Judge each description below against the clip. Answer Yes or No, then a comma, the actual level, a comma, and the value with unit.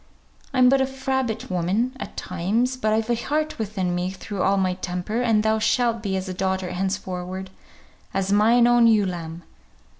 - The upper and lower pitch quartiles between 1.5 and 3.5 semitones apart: No, average, 4.2 semitones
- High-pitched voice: Yes, high, 210 Hz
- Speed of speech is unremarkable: Yes, average, 180 wpm